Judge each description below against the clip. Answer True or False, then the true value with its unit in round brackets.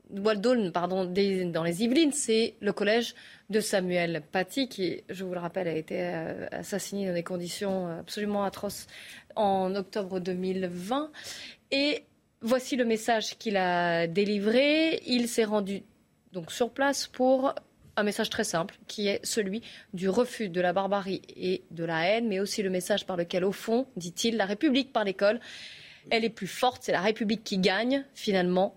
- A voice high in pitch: True (205 Hz)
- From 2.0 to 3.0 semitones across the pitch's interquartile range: False (3.7 semitones)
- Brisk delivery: False (165 wpm)